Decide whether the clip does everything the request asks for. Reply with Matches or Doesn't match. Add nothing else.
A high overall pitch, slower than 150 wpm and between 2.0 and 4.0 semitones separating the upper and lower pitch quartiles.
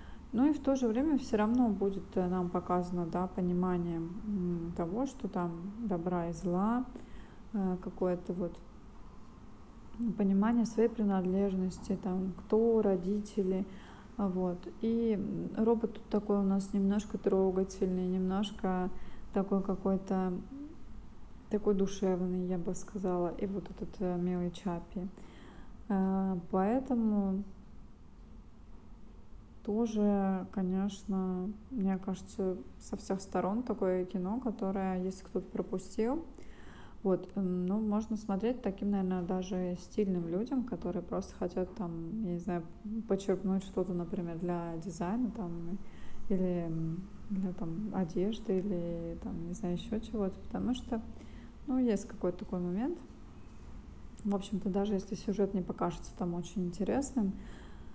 Matches